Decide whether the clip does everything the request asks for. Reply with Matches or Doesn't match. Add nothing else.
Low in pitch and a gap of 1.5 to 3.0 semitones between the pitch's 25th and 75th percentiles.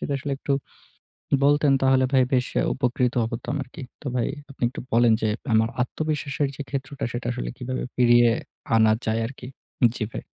Matches